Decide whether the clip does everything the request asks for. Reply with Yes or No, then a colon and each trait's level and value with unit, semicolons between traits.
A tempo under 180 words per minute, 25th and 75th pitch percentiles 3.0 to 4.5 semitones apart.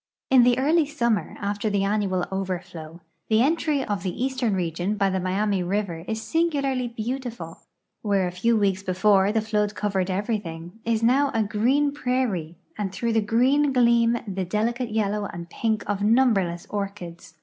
Yes: average, 165 wpm; average, 3.9 semitones